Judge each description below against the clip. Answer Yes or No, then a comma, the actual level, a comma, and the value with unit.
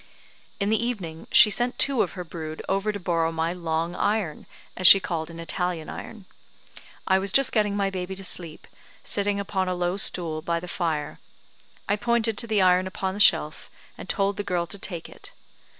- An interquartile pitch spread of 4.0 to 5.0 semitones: No, average, 3.2 semitones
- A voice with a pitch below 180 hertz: No, medium, 185 Hz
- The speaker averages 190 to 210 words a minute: Yes, average, 195 wpm